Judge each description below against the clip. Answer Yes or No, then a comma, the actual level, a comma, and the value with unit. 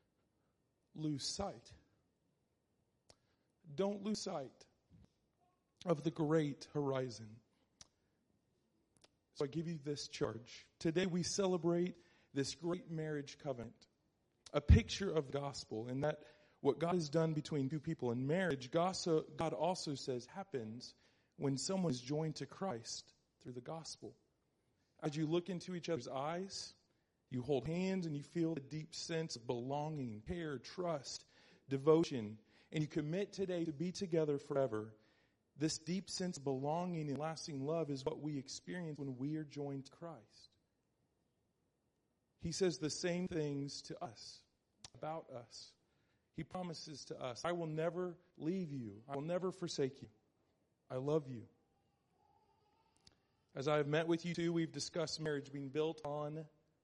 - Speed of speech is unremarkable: Yes, average, 145 wpm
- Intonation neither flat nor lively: Yes, average, 3.9 semitones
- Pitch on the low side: No, medium, 155 Hz